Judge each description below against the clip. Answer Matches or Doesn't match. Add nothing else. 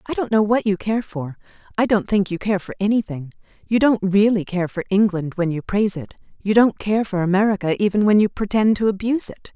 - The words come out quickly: Matches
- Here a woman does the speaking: Matches